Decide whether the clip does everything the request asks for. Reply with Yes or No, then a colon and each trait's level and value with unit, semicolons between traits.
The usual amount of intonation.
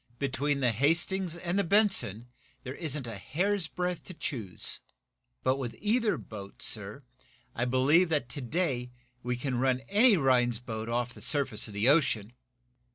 No: wide, 6.1 semitones